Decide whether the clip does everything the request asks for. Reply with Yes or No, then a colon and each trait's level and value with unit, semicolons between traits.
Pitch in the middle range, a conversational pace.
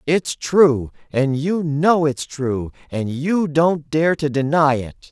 Yes: medium, 150 Hz; average, 165 wpm